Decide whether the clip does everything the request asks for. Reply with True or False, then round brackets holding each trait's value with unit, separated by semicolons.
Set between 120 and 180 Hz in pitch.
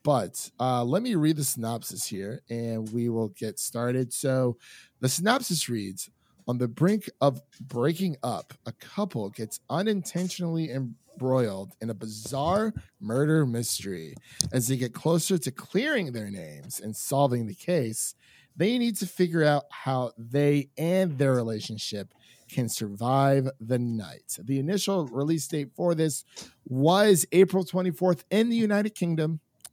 True (140 Hz)